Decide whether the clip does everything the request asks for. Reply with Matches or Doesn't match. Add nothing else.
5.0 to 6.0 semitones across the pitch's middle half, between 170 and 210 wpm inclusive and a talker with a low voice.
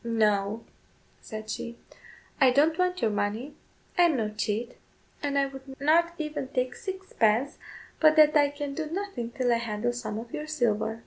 Doesn't match